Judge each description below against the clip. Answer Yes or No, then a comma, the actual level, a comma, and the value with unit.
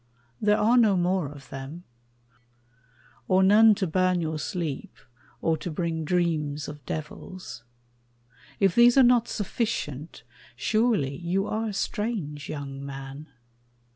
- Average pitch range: No, wide, 5.9 semitones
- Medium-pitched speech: Yes, medium, 175 Hz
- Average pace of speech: No, slow, 130 wpm